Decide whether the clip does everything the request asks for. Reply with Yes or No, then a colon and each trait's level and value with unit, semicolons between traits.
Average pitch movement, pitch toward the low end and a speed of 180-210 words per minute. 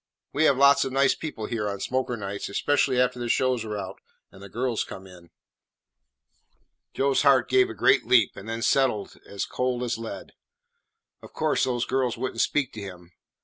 Yes: average, 3.9 semitones; low, 120 Hz; average, 190 wpm